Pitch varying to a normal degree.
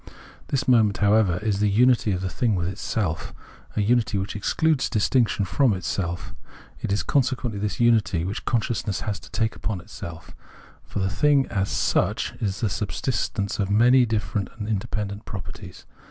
Yes: average, 3.4 semitones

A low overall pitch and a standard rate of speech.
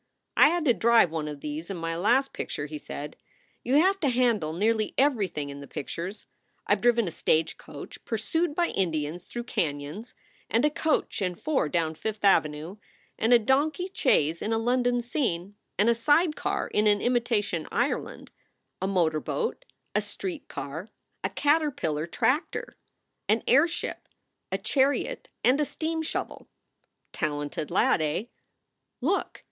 No: high, 220 Hz; average, 155 wpm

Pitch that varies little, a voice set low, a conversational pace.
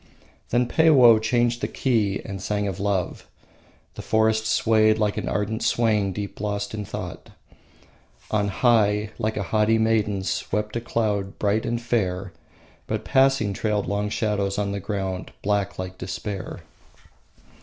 Yes: narrow, 1.8 semitones; low, 105 Hz; average, 145 wpm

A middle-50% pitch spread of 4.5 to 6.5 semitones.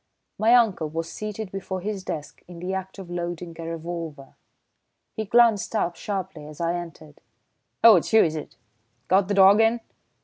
No: average, 3.8 semitones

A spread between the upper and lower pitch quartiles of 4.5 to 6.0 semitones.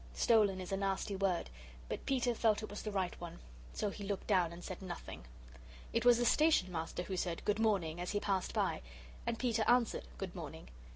No: average, 3.8 semitones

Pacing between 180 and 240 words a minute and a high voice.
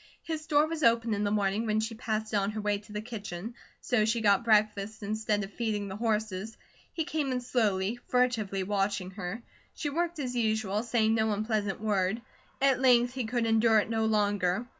Yes: average, 200 wpm; high, 220 Hz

